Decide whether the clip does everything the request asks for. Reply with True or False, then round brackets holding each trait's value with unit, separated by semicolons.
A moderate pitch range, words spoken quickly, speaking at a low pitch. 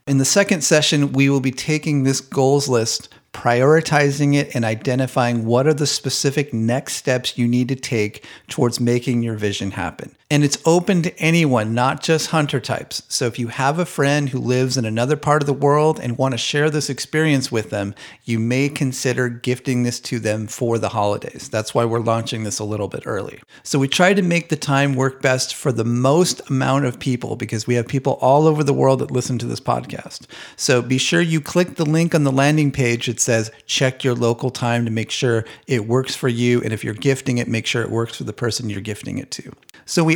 True (3.3 semitones; 225 wpm; 130 Hz)